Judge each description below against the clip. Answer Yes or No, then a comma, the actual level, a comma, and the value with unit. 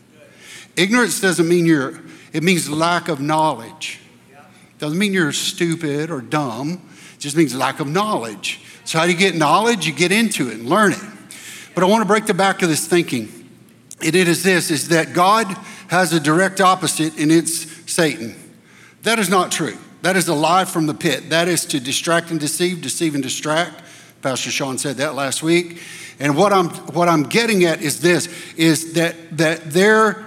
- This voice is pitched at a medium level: Yes, medium, 165 Hz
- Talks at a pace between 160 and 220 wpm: Yes, average, 190 wpm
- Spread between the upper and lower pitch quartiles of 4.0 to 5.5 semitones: No, average, 2.9 semitones